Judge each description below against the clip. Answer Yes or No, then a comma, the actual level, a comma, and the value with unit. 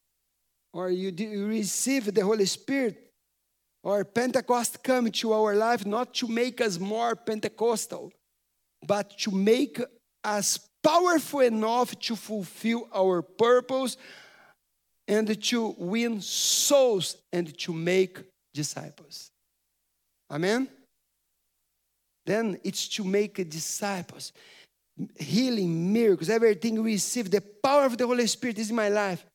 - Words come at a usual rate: No, slow, 115 wpm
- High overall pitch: Yes, high, 215 Hz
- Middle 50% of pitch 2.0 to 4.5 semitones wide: Yes, average, 3.7 semitones